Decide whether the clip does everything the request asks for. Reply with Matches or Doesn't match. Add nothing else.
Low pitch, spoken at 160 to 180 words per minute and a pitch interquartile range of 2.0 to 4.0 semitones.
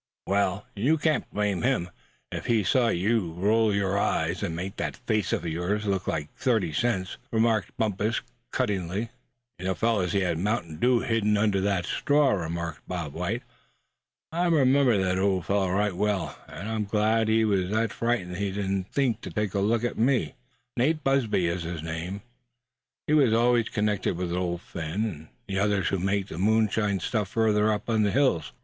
Matches